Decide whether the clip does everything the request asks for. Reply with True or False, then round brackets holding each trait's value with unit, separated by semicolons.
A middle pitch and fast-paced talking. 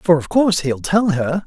True (165 Hz; 245 wpm)